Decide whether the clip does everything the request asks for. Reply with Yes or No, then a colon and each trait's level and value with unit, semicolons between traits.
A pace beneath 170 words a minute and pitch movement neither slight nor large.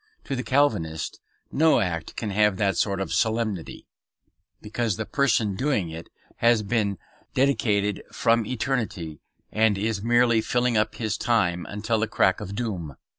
Yes: average, 150 wpm; average, 3.3 semitones